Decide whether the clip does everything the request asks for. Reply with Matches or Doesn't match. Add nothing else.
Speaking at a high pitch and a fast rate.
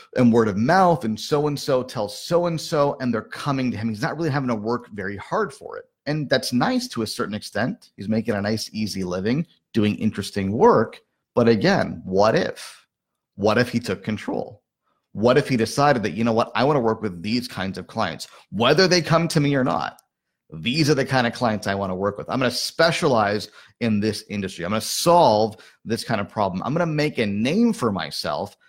Doesn't match